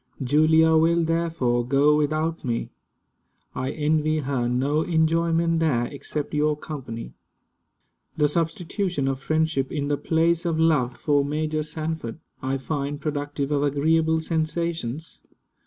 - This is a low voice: No, medium, 155 Hz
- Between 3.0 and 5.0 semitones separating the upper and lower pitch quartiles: No, narrow, 2.4 semitones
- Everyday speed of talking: No, slow, 125 wpm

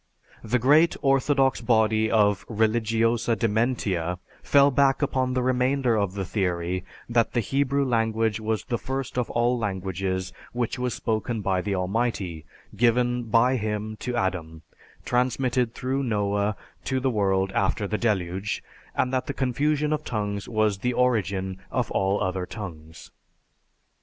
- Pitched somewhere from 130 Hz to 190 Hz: No, low, 110 Hz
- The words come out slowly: No, average, 145 wpm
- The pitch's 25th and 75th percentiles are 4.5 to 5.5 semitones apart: No, average, 4.1 semitones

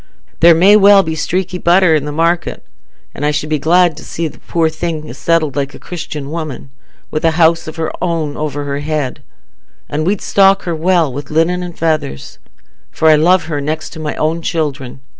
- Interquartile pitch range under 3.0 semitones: Yes, narrow, 2.4 semitones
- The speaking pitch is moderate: Yes, medium, 160 Hz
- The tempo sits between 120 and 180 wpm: No, average, 200 wpm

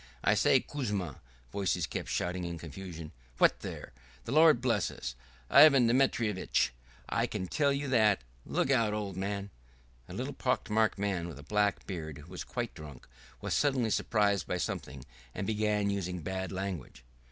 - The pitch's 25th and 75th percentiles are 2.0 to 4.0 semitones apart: No, average, 4.4 semitones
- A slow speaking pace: No, average, 165 wpm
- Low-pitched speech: Yes, low, 100 Hz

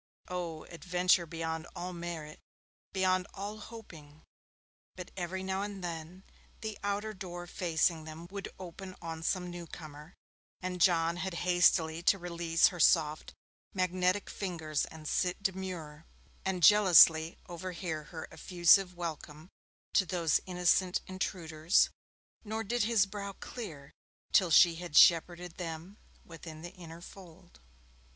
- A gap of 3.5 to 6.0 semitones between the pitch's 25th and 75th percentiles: No, narrow, 2.5 semitones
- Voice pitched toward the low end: No, medium, 175 Hz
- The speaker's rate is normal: No, slow, 130 wpm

